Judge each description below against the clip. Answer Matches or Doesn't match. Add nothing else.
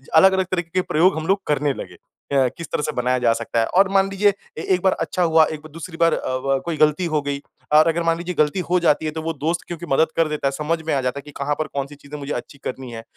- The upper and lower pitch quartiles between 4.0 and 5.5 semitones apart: Doesn't match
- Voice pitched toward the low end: Doesn't match